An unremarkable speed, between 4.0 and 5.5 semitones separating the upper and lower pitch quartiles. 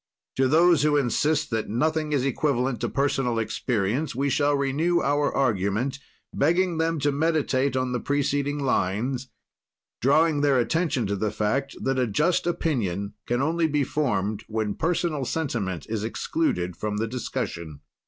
Yes: average, 155 wpm; average, 5.2 semitones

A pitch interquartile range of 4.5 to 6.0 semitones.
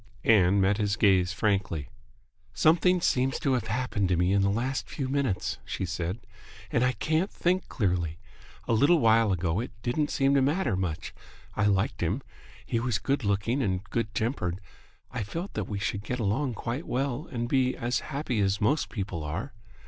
Yes: wide, 5.4 semitones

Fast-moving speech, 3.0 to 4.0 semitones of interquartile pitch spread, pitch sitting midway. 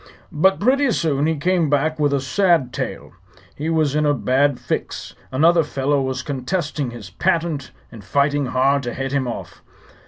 No: average, 175 wpm; average, 3.4 semitones; medium, 145 Hz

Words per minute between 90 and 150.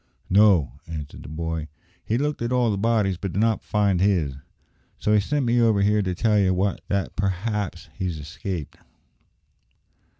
No: average, 165 wpm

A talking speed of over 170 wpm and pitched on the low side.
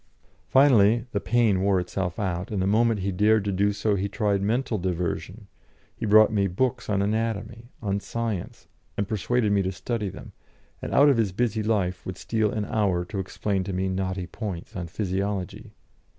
Yes: average, 185 wpm; low, 100 Hz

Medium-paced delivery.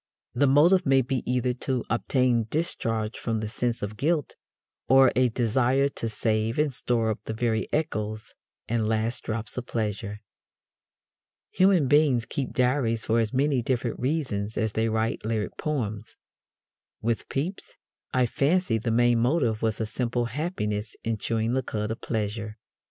Yes: average, 155 wpm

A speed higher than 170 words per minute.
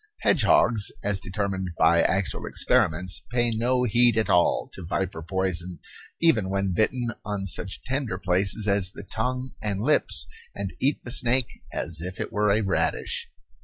No: average, 160 wpm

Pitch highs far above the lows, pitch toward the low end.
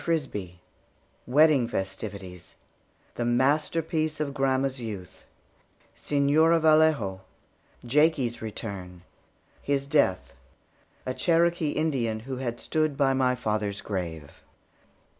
Yes: wide, 6.6 semitones; low, 130 Hz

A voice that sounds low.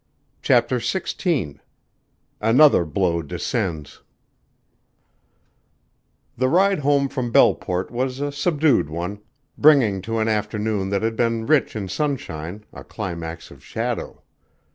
Yes: low, 115 Hz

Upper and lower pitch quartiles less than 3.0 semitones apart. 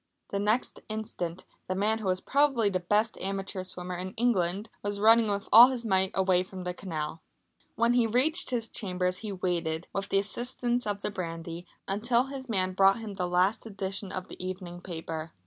No: average, 3.5 semitones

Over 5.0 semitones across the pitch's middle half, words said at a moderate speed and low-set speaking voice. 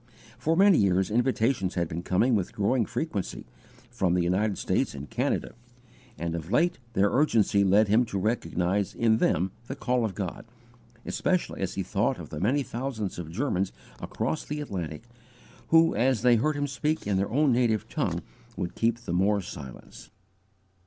Yes: wide, 5.5 semitones; average, 175 wpm; low, 105 Hz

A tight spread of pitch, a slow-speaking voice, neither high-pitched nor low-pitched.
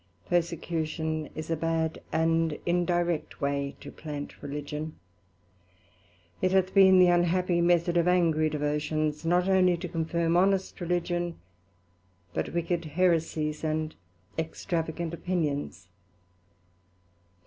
Yes: narrow, 2.1 semitones; slow, 105 wpm; medium, 165 Hz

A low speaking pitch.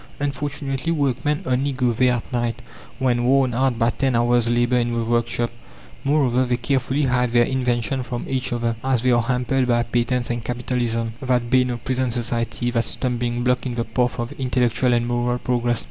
Yes: low, 125 Hz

